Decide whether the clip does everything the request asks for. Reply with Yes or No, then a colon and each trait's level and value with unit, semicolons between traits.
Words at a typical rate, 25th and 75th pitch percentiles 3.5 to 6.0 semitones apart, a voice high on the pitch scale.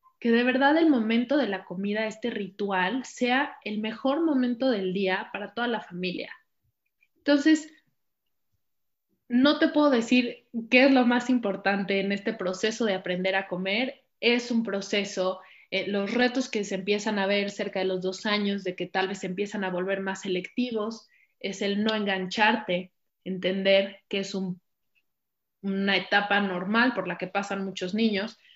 Yes: average, 170 wpm; average, 4.1 semitones; high, 205 Hz